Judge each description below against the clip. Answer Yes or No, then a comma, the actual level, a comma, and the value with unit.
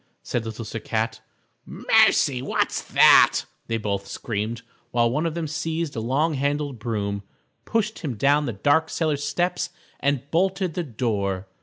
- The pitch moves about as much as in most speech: No, wide, 6.1 semitones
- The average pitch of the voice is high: No, medium, 140 Hz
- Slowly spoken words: No, average, 155 wpm